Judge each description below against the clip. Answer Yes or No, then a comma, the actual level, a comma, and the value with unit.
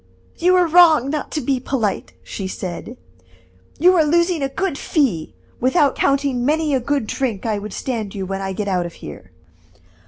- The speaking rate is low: No, average, 185 wpm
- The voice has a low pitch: No, very high, 265 Hz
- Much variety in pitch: Yes, wide, 7.2 semitones